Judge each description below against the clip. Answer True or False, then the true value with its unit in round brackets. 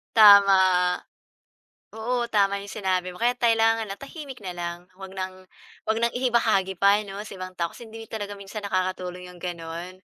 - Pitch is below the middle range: False (200 Hz)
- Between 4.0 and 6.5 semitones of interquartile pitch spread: False (3.4 semitones)